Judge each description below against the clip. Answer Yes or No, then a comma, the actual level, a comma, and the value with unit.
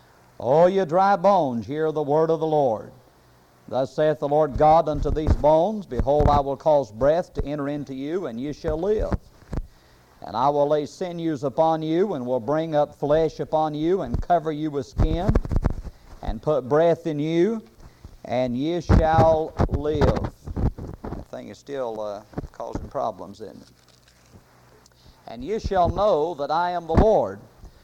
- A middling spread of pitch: Yes, average, 3.5 semitones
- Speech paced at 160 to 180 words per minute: Yes, average, 170 wpm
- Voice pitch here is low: No, medium, 150 Hz